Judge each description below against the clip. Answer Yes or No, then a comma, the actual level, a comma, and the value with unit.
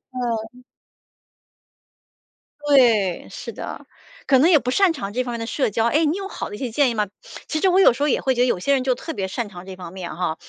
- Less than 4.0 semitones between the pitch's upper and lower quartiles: No, average, 5.3 semitones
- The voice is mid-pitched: No, high, 245 Hz